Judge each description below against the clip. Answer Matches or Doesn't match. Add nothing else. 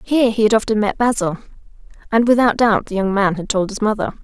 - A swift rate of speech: Matches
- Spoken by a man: Doesn't match